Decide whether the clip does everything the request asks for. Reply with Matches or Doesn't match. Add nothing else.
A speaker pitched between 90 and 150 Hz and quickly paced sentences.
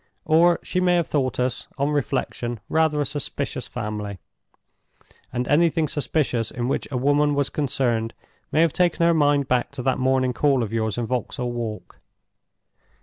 Doesn't match